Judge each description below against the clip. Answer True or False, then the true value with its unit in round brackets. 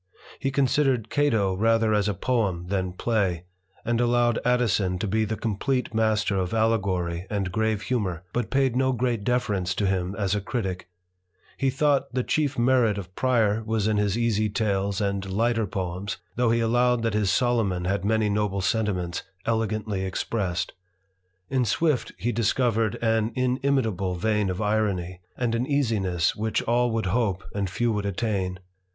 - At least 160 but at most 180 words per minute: True (165 wpm)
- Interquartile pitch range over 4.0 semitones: False (3.6 semitones)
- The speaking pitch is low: True (110 Hz)